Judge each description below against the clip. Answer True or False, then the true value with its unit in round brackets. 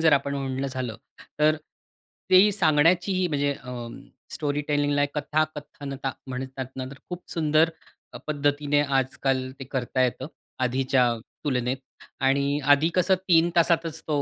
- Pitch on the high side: False (145 Hz)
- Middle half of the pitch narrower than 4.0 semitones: True (2.8 semitones)